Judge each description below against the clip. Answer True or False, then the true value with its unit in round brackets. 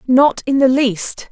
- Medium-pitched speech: False (260 Hz)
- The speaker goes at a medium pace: True (185 wpm)